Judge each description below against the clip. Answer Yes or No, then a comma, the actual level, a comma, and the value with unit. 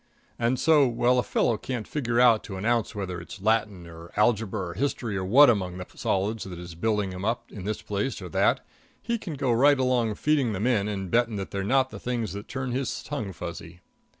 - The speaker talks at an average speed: No, fast, 225 wpm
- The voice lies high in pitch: No, low, 110 Hz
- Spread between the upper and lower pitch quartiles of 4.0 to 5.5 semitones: Yes, average, 4.4 semitones